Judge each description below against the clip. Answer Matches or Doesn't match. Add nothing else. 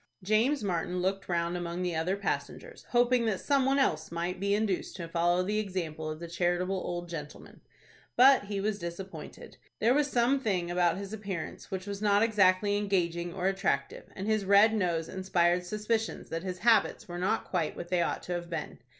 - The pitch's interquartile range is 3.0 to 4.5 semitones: Matches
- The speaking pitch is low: Doesn't match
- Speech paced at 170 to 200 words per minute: Matches